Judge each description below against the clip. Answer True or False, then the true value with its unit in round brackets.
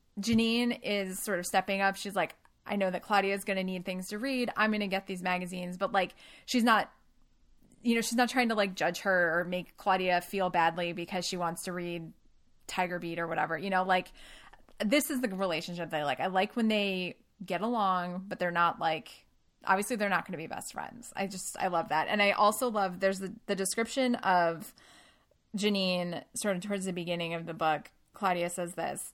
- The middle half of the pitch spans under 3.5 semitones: True (2.7 semitones)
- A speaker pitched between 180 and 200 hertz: True (190 Hz)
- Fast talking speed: True (220 wpm)